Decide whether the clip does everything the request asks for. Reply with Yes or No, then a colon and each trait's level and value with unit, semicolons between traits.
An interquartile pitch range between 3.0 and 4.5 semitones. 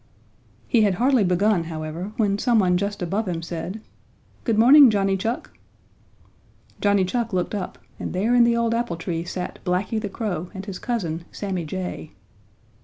Yes: average, 3.9 semitones